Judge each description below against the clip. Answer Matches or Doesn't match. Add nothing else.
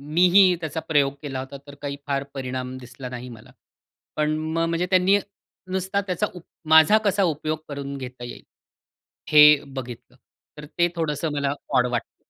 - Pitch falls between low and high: Matches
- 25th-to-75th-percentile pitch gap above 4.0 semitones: Matches